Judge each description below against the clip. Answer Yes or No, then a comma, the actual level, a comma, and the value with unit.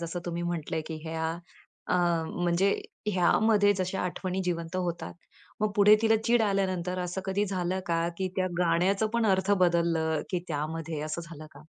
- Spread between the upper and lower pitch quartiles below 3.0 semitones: Yes, narrow, 2.4 semitones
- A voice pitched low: No, medium, 175 Hz